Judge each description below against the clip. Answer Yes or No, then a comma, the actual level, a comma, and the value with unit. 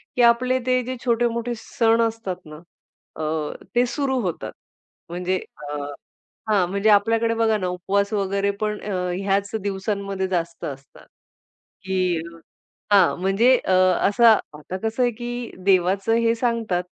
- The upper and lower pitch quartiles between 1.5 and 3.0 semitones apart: No, average, 3.7 semitones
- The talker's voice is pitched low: No, high, 200 Hz